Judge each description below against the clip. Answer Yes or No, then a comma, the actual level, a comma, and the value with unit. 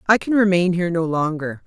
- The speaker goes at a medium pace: No, fast, 215 wpm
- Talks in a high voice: No, medium, 180 Hz